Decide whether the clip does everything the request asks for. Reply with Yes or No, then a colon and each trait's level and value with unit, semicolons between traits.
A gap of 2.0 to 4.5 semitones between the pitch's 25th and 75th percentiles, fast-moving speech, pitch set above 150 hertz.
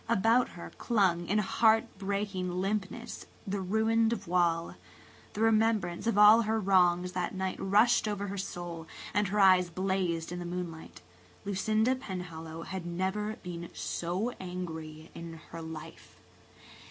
No: average, 3.3 semitones; average, 140 wpm; high, 190 Hz